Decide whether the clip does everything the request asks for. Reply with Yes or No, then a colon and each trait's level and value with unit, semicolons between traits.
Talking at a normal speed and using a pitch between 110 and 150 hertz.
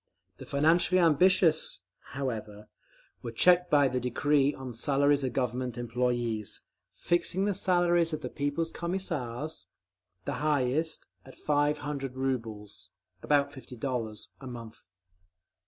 No: slow, 115 wpm; medium, 140 Hz